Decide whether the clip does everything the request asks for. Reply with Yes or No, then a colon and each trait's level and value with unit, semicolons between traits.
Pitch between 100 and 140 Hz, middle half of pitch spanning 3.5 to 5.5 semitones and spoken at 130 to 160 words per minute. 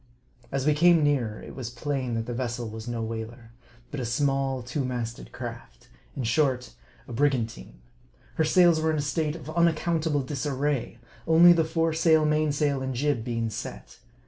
No: low, 135 Hz; average, 4.5 semitones; average, 170 wpm